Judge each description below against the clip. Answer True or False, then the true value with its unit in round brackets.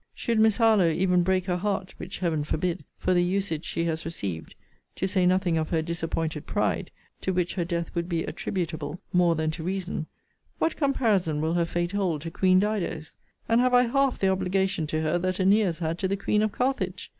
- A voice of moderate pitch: True (180 Hz)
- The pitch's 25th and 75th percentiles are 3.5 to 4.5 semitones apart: False (3.0 semitones)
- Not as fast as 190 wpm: False (205 wpm)